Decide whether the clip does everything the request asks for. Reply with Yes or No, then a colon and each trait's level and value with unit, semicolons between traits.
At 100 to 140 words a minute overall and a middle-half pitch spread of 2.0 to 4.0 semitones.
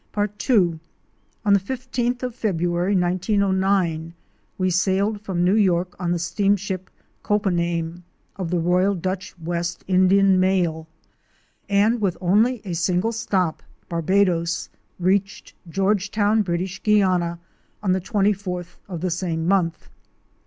Yes: slow, 135 wpm; narrow, 2.6 semitones